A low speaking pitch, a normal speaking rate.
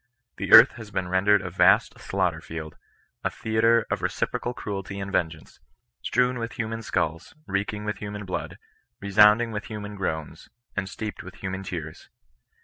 Yes: low, 100 Hz; average, 175 wpm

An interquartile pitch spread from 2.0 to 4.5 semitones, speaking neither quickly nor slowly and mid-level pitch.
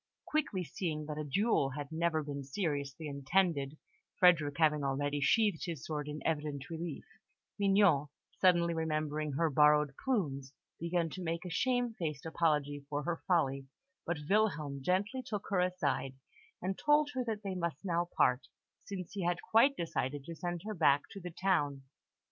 Yes: average, 4.2 semitones; average, 160 wpm; medium, 165 Hz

